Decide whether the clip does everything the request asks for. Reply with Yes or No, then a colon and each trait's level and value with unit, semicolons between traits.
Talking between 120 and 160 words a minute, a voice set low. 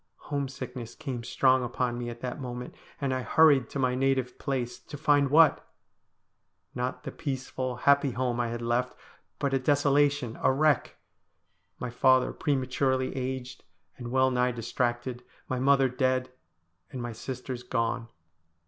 Yes: average, 150 wpm; low, 130 Hz